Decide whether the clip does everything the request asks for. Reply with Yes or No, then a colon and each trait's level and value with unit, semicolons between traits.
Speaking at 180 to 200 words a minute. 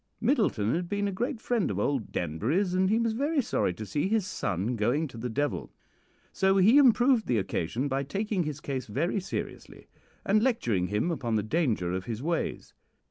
Yes: average, 190 wpm